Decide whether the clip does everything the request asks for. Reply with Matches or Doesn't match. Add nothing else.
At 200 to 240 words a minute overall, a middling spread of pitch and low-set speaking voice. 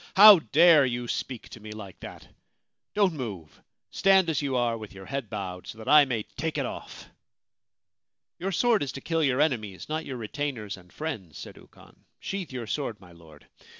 Doesn't match